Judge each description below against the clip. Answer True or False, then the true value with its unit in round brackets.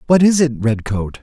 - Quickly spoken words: False (195 wpm)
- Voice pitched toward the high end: False (135 Hz)